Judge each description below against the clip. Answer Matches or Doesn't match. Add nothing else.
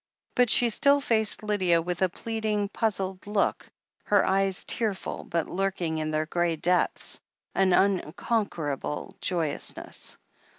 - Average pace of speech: Doesn't match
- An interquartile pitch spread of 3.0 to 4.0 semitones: Matches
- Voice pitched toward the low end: Doesn't match